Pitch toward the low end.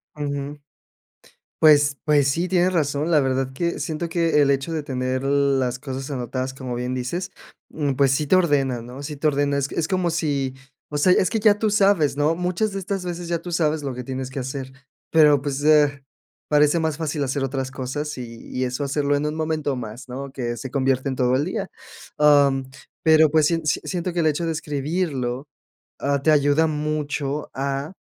No: medium, 145 Hz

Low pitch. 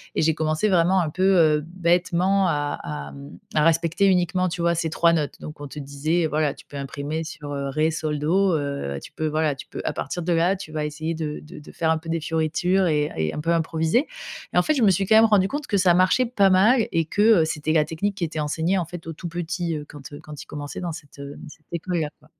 No: medium, 160 Hz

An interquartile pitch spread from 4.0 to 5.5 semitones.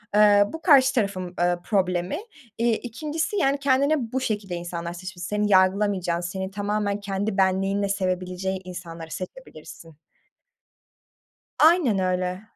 No: average, 3.6 semitones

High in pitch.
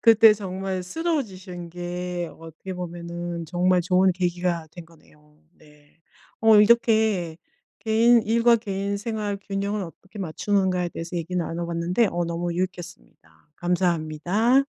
No: medium, 180 Hz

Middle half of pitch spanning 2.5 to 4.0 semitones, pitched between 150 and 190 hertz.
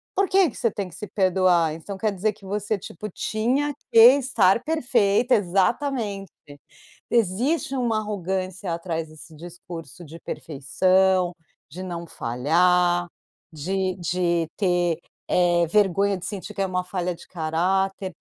Yes: average, 3.3 semitones; medium, 185 Hz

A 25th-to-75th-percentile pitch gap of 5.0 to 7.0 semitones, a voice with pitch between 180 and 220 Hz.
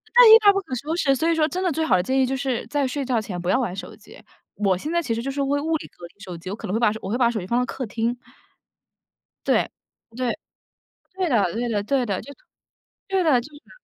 No: wide, 5.5 semitones; very high, 255 Hz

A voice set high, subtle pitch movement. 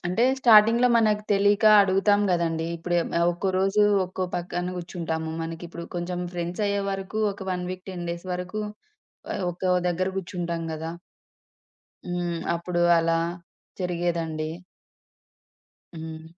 No: medium, 180 Hz; narrow, 2.3 semitones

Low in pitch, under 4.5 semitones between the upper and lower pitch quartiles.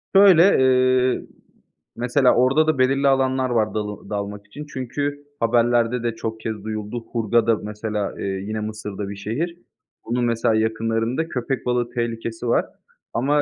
Yes: low, 115 Hz; average, 3.0 semitones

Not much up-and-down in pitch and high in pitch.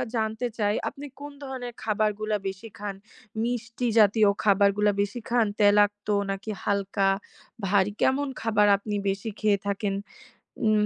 Yes: narrow, 1.9 semitones; high, 210 Hz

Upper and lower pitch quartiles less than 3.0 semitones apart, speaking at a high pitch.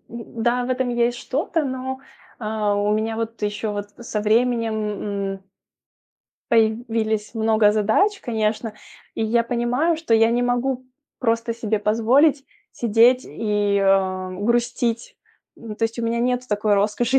Yes: narrow, 2.5 semitones; high, 230 Hz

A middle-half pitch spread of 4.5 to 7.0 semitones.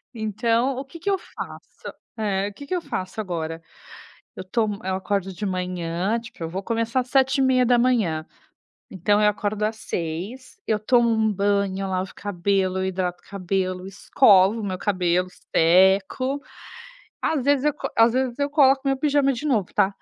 Yes: average, 5.2 semitones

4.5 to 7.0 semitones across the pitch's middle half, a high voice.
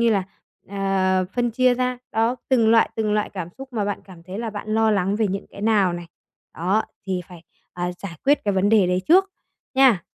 No: average, 3.5 semitones; high, 205 Hz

